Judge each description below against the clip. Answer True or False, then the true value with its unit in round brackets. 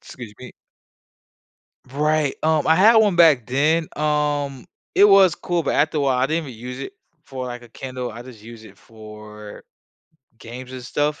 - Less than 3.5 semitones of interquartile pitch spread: False (4.3 semitones)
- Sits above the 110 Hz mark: True (135 Hz)